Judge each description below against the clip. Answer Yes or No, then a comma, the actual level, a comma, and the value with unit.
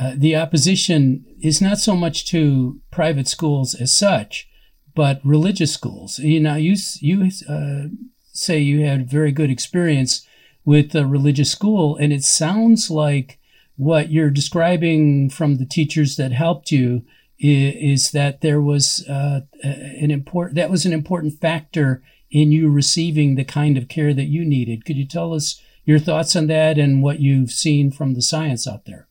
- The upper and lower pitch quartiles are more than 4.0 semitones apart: No, average, 2.7 semitones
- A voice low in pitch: No, medium, 150 Hz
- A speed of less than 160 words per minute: No, average, 170 wpm